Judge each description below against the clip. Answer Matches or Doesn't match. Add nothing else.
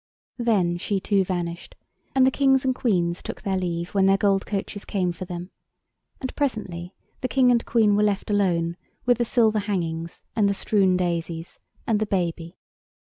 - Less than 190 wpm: Matches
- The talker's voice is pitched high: Matches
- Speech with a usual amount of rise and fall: Matches